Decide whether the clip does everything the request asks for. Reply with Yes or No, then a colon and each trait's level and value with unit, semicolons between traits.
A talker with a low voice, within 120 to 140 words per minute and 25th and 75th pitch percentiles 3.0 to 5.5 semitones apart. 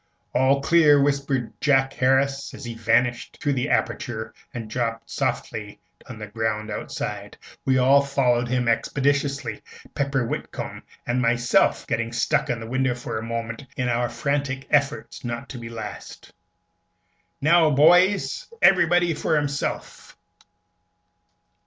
Yes: low, 130 Hz; slow, 135 wpm; average, 3.3 semitones